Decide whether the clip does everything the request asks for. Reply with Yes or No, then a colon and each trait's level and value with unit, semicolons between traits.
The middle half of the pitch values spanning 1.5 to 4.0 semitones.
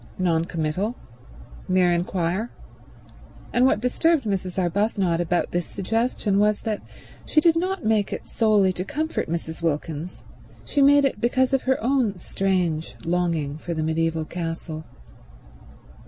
No: wide, 5.6 semitones